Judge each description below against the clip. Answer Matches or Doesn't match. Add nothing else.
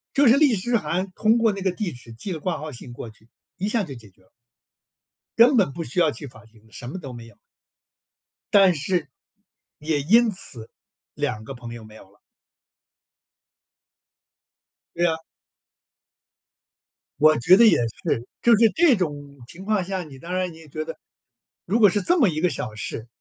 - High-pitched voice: Doesn't match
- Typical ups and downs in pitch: Doesn't match